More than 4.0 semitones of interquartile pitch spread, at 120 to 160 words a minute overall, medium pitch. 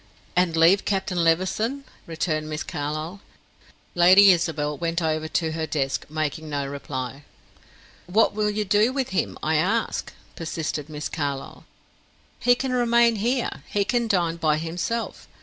Yes: average, 5.1 semitones; average, 145 wpm; medium, 170 Hz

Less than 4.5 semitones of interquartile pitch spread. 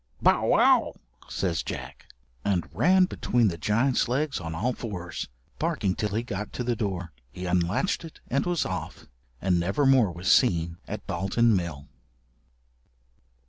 No: wide, 5.6 semitones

